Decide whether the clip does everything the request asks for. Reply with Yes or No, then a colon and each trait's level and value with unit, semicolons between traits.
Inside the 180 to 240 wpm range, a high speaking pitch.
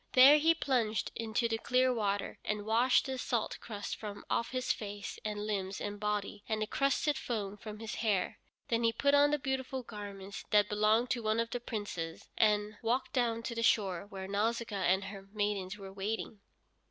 Yes: average, 190 wpm; high, 215 Hz